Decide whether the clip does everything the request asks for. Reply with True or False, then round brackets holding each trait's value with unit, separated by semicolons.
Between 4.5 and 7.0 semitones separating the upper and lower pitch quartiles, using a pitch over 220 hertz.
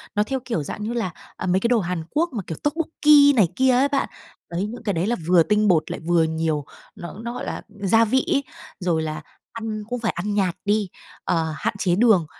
False (5.6 semitones; 210 Hz)